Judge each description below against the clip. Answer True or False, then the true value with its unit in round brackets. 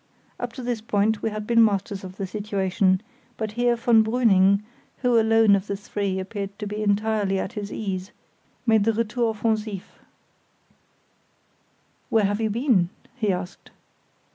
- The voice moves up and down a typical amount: False (2.2 semitones)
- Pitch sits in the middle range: False (210 Hz)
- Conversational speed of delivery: True (155 wpm)